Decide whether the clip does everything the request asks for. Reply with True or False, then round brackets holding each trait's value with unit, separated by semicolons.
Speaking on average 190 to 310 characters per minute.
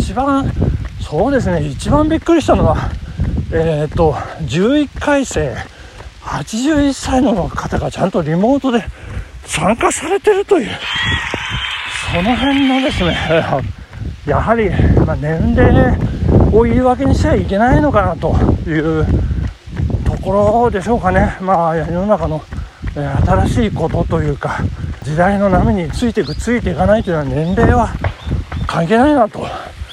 True (265 characters per minute)